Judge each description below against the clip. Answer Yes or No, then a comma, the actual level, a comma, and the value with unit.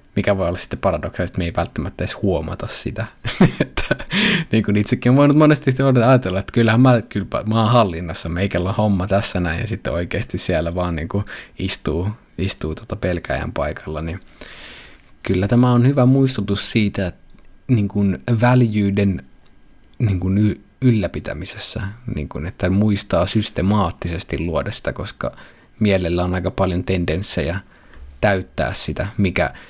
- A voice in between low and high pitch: No, low, 100 Hz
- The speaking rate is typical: Yes, average, 135 wpm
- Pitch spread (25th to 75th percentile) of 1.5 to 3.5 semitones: No, average, 3.9 semitones